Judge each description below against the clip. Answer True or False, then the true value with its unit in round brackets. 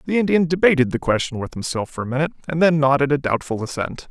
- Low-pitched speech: False (145 Hz)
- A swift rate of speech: True (235 wpm)